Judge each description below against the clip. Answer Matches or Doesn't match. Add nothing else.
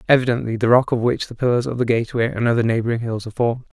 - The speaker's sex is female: Doesn't match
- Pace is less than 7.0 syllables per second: Doesn't match